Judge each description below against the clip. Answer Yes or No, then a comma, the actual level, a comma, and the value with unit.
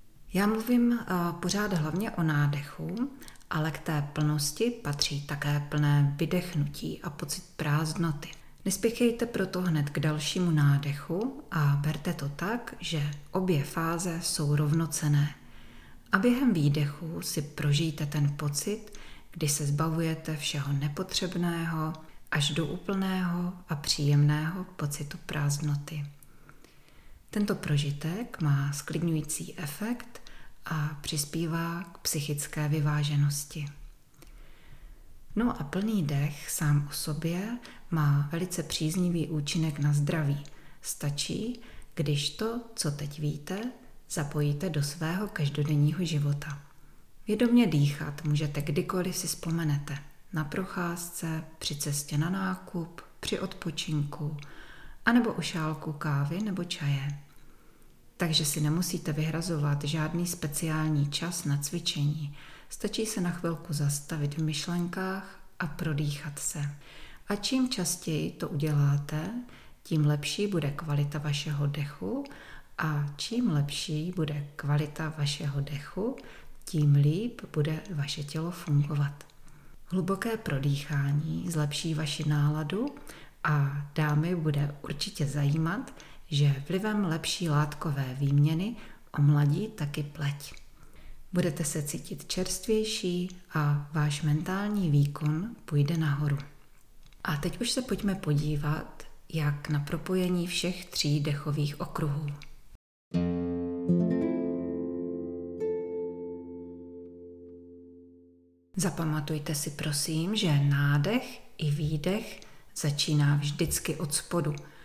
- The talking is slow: Yes, slow, 105 wpm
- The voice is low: No, medium, 155 Hz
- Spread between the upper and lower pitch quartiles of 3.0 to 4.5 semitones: Yes, average, 3.3 semitones